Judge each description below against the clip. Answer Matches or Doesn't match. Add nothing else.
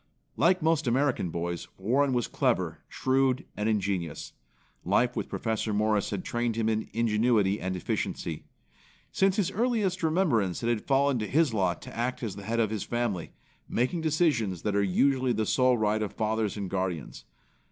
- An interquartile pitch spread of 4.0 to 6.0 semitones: Matches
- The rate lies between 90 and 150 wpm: Doesn't match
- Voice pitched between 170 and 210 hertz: Doesn't match